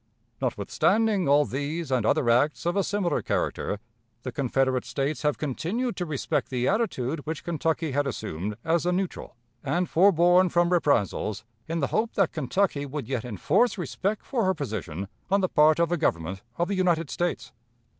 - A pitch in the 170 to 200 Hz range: No, medium, 155 Hz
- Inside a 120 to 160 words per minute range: No, average, 175 wpm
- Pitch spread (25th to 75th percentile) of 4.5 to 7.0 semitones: Yes, wide, 5.4 semitones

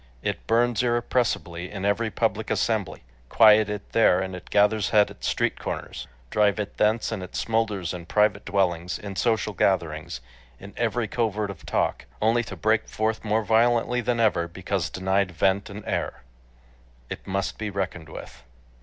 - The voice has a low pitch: Yes, low, 105 Hz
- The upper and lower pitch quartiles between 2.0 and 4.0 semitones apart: Yes, average, 2.8 semitones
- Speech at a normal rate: Yes, average, 165 wpm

